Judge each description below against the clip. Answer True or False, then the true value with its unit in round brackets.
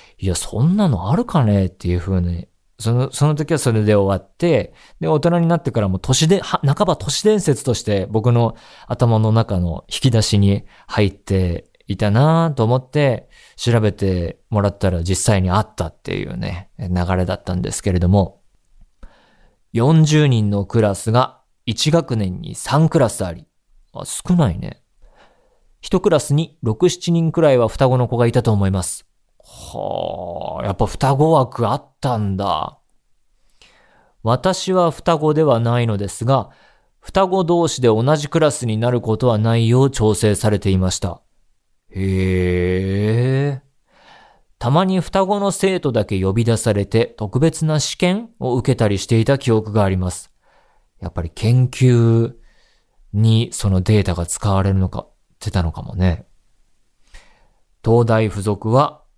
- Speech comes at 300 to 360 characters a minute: False (270 characters per minute)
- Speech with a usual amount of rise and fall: False (6.6 semitones)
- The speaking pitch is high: False (115 Hz)